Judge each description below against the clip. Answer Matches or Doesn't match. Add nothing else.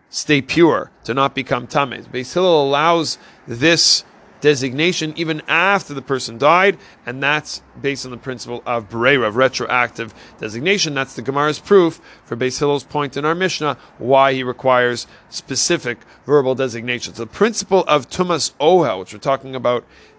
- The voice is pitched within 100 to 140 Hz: Matches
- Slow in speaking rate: Doesn't match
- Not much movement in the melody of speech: Doesn't match